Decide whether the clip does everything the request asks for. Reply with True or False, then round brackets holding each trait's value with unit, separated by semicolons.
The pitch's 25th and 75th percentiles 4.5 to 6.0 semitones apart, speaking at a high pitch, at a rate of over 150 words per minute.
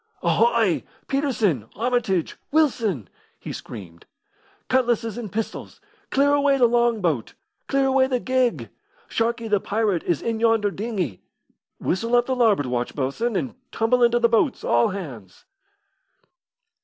False (5.3 semitones; 230 Hz; 135 wpm)